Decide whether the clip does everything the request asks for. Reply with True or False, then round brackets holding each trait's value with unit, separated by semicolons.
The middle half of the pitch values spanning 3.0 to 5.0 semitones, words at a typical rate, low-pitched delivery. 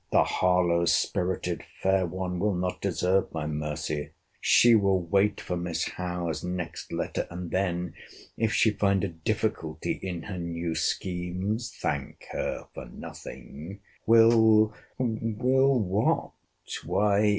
False (3.4 semitones; 115 wpm; 90 Hz)